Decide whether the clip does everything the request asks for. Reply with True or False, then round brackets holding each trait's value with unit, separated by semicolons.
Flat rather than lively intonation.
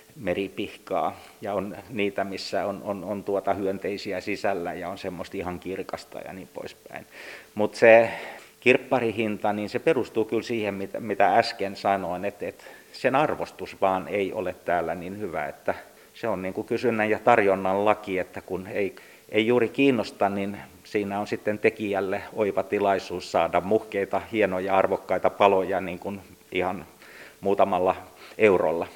True (2.0 semitones)